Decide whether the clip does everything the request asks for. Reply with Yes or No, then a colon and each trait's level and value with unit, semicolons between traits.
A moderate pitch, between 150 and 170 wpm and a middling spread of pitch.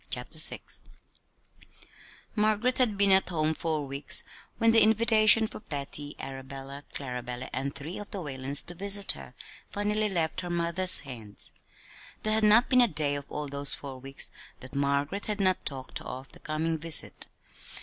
No: medium, 160 Hz; average, 165 wpm; wide, 6.8 semitones